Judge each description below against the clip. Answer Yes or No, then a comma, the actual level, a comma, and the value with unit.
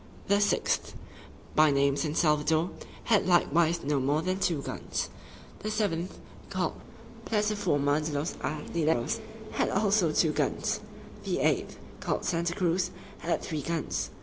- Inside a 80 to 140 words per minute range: Yes, slow, 135 wpm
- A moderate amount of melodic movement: Yes, average, 3.7 semitones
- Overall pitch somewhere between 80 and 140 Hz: No, medium, 165 Hz